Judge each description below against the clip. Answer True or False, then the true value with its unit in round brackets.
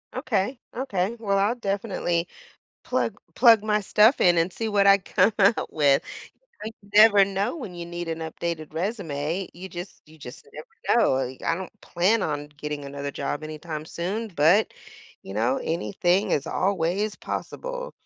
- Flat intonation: False (5.0 semitones)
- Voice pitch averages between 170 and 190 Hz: True (185 Hz)